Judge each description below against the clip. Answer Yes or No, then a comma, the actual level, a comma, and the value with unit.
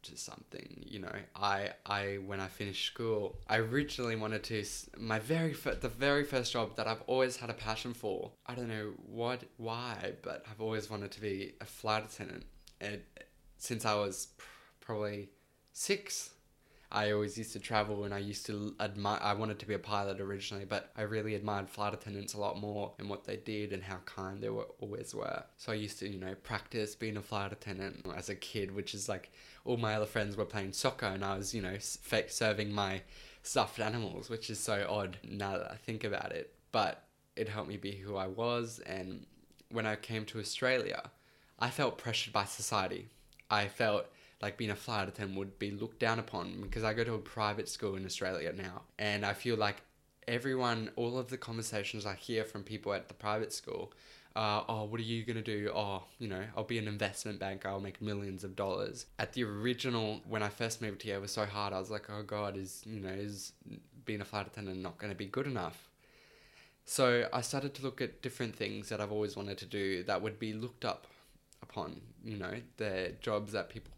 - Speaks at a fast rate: Yes, fast, 215 wpm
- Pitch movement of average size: No, narrow, 2.2 semitones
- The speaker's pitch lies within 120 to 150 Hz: No, low, 105 Hz